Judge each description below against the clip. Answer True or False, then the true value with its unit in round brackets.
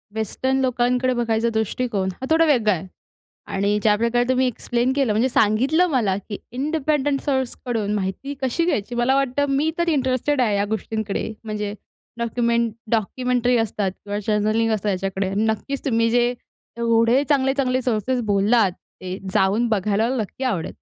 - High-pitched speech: True (235 Hz)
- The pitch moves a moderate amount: True (3.7 semitones)